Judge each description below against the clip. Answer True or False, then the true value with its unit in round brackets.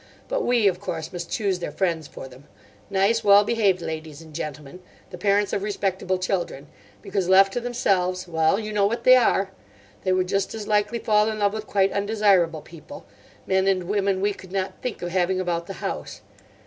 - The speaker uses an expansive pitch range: False (2.8 semitones)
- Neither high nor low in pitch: False (195 Hz)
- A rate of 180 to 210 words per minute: True (185 wpm)